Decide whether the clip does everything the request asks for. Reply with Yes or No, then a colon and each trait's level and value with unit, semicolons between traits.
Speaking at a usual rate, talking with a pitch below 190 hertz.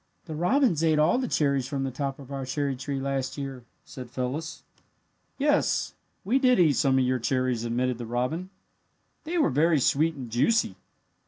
Yes: average, 180 wpm; medium, 140 Hz